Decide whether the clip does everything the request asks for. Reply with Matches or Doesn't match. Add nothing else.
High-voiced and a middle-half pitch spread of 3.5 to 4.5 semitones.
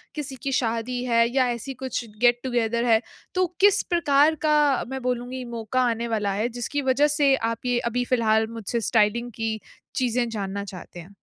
Doesn't match